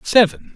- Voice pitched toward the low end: No, high, 210 Hz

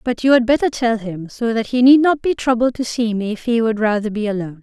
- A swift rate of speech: Yes, fast, 285 wpm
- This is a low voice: No, high, 230 Hz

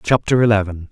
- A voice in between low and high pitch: No, low, 105 Hz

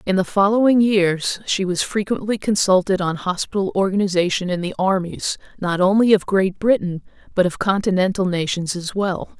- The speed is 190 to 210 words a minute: No, average, 160 wpm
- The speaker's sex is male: No, female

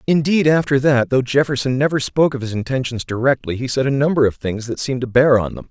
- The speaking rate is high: Yes, fast, 240 wpm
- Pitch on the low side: Yes, low, 130 Hz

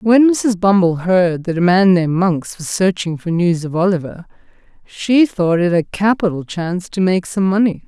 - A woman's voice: Yes, female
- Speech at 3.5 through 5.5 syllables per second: Yes, 4.7 syllables/s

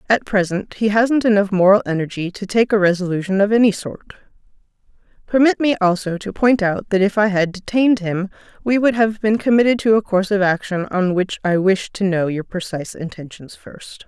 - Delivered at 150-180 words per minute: No, average, 195 wpm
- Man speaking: No, female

